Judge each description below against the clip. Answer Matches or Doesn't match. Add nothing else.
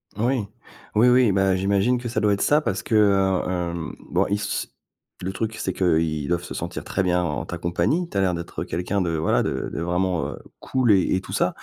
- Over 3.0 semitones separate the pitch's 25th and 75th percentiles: Matches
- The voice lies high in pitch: Doesn't match